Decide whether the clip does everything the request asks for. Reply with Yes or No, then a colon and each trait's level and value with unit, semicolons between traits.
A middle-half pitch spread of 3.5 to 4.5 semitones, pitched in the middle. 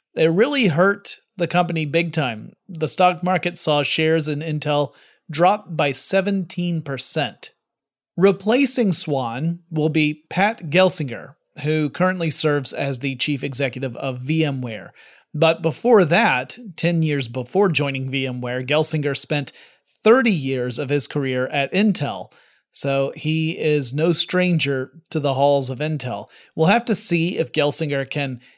Yes: average, 4.0 semitones; medium, 155 Hz